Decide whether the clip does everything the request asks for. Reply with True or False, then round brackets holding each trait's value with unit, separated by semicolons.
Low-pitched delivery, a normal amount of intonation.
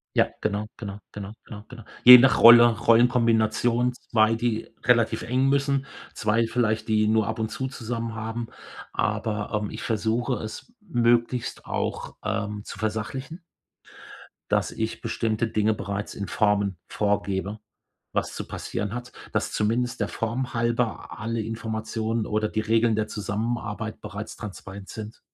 False (110 Hz; 1.9 semitones)